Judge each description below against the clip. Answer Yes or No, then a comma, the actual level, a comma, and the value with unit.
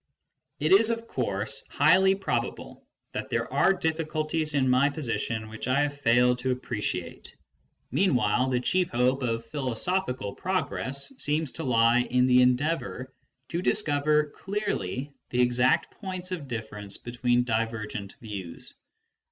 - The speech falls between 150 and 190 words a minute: No, slow, 135 wpm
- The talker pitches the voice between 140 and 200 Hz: No, low, 130 Hz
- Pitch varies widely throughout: No, average, 4.9 semitones